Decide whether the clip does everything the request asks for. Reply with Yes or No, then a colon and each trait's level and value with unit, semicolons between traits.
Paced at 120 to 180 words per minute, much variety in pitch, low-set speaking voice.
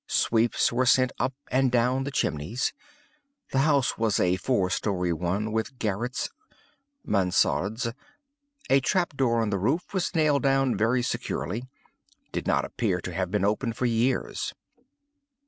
No: average, 145 wpm; average, 4.4 semitones; low, 120 Hz